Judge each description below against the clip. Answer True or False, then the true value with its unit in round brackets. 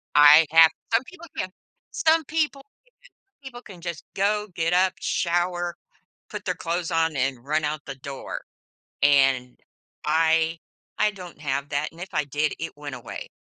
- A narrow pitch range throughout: False (4.1 semitones)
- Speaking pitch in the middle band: True (165 Hz)